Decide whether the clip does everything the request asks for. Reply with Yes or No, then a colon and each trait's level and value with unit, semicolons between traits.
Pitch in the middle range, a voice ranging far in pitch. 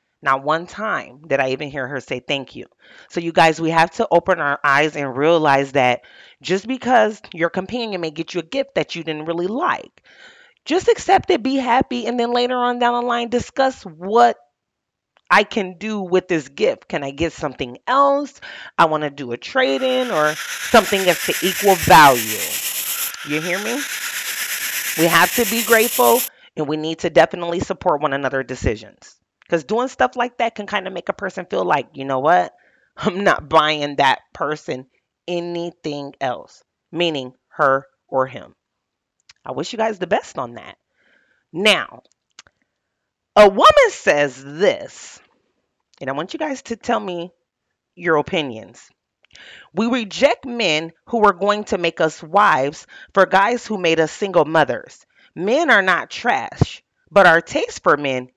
Yes: medium, 175 Hz; wide, 7.7 semitones